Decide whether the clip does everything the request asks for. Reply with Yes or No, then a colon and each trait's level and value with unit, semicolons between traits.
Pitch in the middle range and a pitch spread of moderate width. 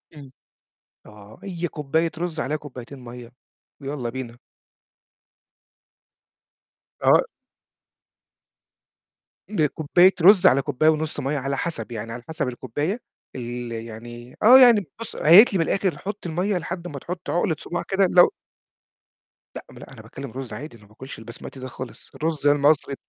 No: medium, 145 Hz; wide, 5.8 semitones